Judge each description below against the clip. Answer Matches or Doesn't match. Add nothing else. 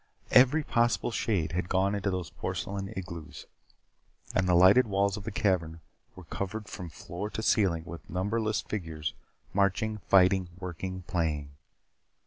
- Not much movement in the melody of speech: Doesn't match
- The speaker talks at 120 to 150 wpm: Matches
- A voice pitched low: Matches